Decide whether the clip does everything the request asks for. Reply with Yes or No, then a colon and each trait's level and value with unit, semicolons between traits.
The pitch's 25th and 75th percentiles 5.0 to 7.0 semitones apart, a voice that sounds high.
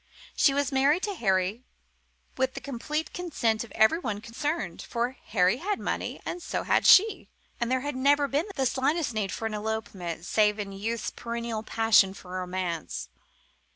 Yes: wide, 5.4 semitones; high, 235 Hz